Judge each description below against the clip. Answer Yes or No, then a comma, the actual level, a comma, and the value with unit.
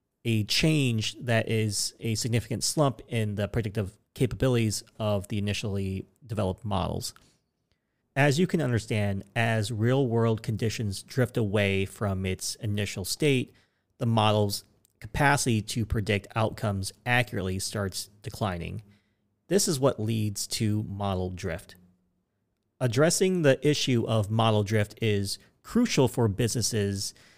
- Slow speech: Yes, slow, 125 wpm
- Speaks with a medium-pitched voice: No, low, 110 Hz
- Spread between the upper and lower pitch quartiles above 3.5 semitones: No, average, 3.1 semitones